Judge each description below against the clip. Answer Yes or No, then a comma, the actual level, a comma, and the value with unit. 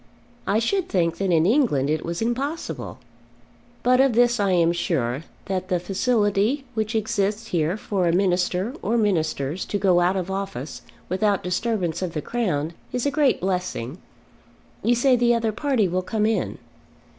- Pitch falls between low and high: No, high, 195 Hz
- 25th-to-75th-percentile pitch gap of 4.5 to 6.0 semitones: Yes, average, 4.9 semitones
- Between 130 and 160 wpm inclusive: No, average, 170 wpm